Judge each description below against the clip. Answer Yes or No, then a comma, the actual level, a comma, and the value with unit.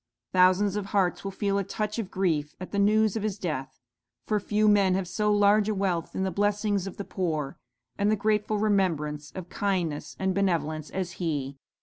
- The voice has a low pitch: No, high, 195 Hz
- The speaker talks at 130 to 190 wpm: No, average, 200 wpm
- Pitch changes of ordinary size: Yes, average, 3.0 semitones